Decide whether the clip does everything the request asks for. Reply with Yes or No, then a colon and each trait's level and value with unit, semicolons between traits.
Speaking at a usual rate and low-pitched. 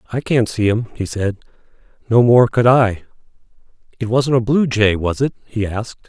Yes: average, 190 wpm; low, 115 Hz